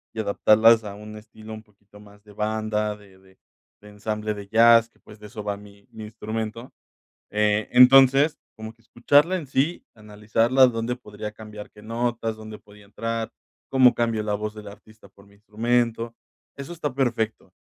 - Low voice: Yes, low, 110 Hz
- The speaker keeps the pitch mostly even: Yes, narrow, 1.8 semitones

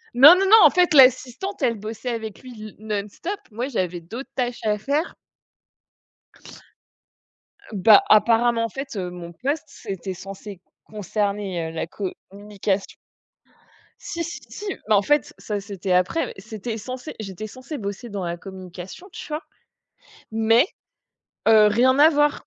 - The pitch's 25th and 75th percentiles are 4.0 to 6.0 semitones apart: Yes, average, 4.9 semitones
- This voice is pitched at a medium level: No, high, 220 Hz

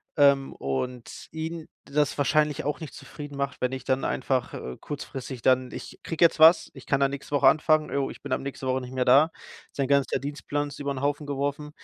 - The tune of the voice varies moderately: No, narrow, 2.1 semitones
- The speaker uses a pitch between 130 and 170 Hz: Yes, medium, 140 Hz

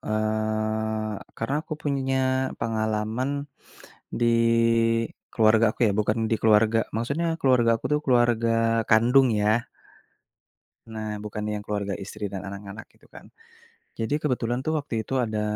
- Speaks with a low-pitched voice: Yes, low, 110 Hz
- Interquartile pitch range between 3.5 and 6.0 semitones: No, narrow, 2.5 semitones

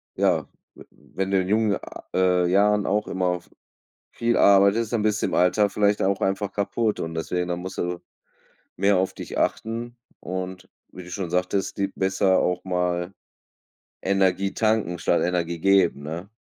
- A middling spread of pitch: No, narrow, 2.2 semitones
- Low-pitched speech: Yes, very low, 95 Hz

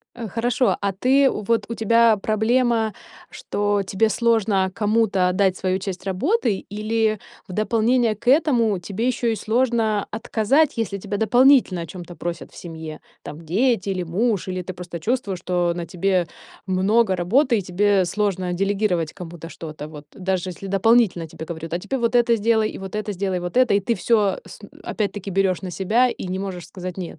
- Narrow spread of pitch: No, average, 3.9 semitones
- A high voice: Yes, high, 200 Hz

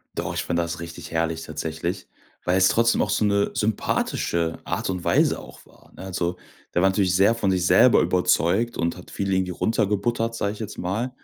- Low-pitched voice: Yes, very low, 95 Hz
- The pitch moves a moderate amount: Yes, average, 3.4 semitones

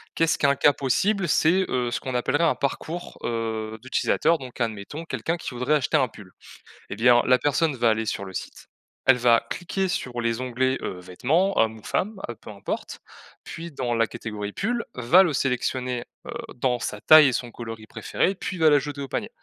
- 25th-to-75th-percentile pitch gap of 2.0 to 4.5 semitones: No, wide, 5.4 semitones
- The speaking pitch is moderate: No, low, 130 Hz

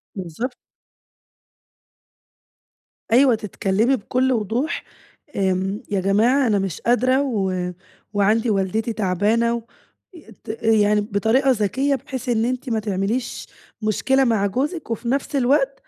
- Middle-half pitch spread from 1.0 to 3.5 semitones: No, average, 4.1 semitones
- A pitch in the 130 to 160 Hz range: No, high, 225 Hz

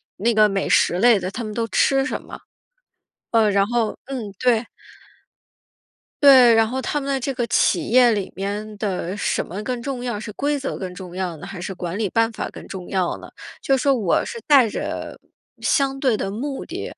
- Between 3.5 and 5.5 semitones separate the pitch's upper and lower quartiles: Yes, average, 4.6 semitones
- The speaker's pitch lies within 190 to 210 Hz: No, high, 225 Hz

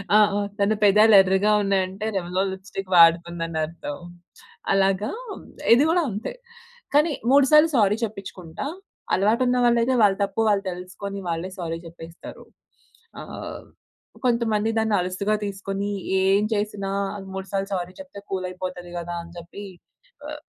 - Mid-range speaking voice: No, high, 195 Hz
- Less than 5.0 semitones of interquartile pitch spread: Yes, average, 2.7 semitones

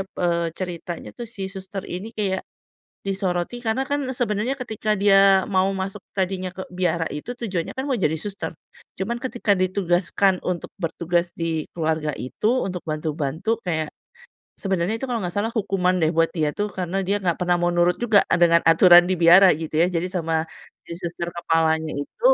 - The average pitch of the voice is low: No, medium, 185 Hz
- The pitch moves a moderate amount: Yes, average, 3.0 semitones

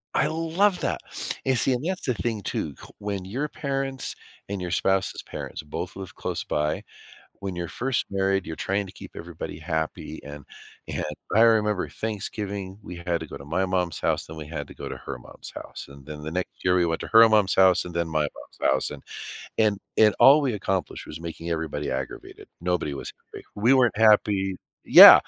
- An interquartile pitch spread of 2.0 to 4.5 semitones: No, average, 4.9 semitones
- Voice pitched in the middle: No, very low, 95 Hz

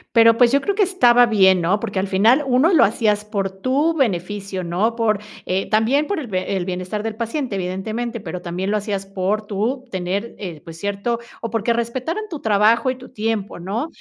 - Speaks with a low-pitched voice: No, high, 215 Hz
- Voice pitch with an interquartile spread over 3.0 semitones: Yes, average, 3.9 semitones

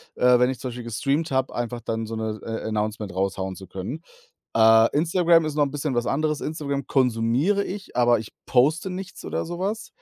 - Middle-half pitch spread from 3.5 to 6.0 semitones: Yes, wide, 5.6 semitones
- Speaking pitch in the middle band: No, low, 125 Hz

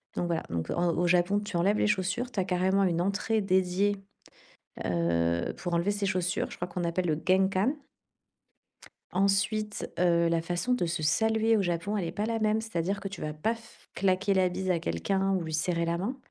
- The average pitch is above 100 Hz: Yes, medium, 185 Hz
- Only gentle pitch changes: No, average, 3.1 semitones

